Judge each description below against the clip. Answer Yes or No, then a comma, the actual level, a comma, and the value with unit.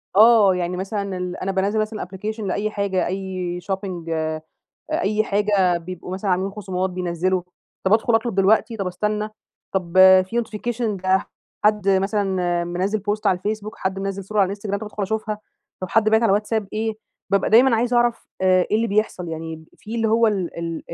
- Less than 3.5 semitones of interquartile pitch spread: Yes, average, 2.7 semitones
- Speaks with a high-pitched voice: Yes, high, 195 Hz